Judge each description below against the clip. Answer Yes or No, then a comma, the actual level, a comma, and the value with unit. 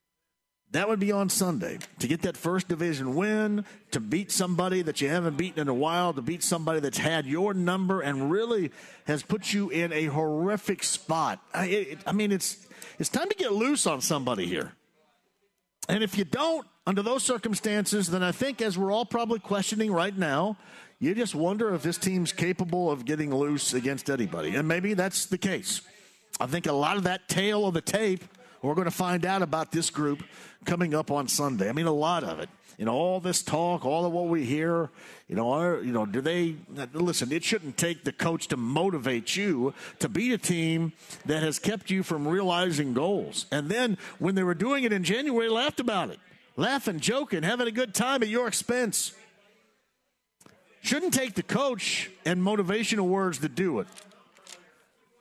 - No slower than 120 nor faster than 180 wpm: No, average, 195 wpm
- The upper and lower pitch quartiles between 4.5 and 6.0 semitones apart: No, average, 4.1 semitones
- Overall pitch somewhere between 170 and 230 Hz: Yes, medium, 185 Hz